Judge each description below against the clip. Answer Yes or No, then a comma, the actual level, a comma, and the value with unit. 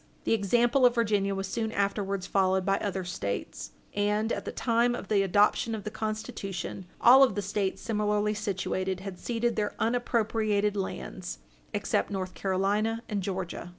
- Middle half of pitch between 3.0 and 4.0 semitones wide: No, narrow, 2.5 semitones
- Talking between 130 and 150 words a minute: No, average, 160 wpm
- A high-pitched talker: Yes, high, 205 Hz